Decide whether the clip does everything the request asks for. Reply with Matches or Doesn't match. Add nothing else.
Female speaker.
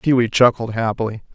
Doesn't match